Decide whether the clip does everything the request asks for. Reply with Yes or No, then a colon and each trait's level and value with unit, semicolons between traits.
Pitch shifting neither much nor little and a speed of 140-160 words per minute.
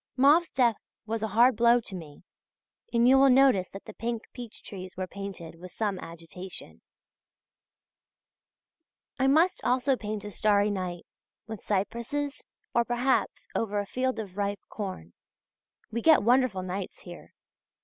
Yes: average, 4.6 semitones; average, 150 wpm